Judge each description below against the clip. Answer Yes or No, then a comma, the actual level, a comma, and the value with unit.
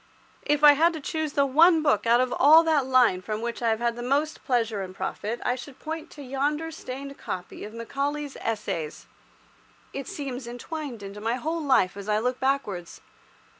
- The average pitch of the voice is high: Yes, very high, 255 Hz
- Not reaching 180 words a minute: No, average, 195 wpm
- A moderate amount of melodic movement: Yes, average, 4.5 semitones